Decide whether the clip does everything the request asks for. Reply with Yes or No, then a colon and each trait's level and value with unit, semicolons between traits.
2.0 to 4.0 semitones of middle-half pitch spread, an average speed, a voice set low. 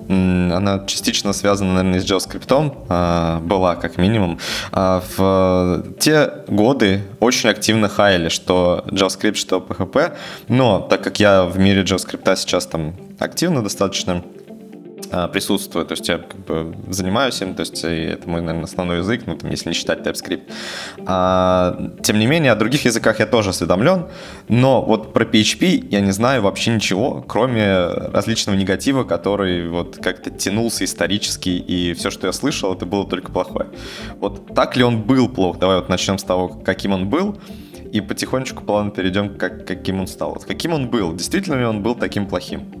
No: average, 3.0 semitones; fast, 165 wpm; very low, 95 Hz